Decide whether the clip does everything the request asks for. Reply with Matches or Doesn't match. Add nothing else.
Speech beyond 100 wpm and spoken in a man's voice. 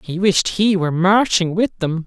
Matches